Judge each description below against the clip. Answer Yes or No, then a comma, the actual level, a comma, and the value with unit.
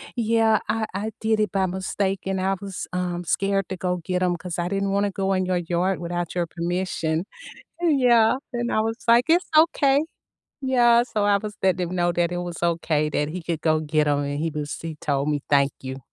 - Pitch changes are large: No, average, 4.0 semitones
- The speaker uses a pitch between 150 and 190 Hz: Yes, medium, 185 Hz